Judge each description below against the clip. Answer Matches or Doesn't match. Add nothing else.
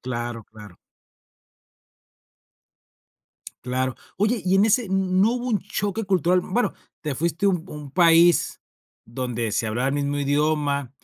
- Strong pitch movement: Matches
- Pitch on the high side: Doesn't match